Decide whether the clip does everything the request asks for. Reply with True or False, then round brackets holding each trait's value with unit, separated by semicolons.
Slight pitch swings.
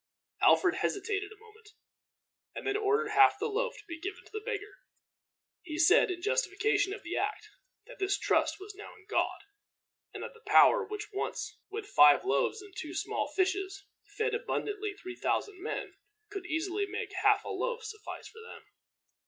True (1.9 semitones)